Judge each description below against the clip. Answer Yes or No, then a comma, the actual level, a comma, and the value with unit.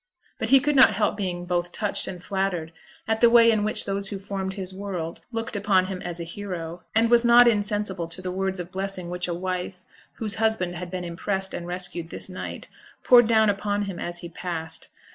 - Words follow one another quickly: Yes, fast, 215 wpm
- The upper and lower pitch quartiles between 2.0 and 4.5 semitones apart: Yes, average, 2.9 semitones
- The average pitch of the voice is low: No, high, 190 Hz